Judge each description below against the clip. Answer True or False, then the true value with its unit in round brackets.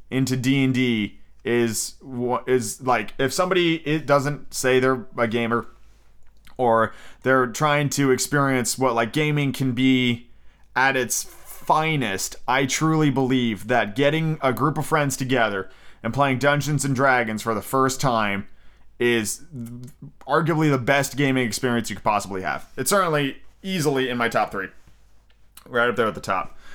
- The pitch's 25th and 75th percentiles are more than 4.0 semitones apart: False (3.3 semitones)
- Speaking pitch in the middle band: False (130 Hz)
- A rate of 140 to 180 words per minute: True (155 wpm)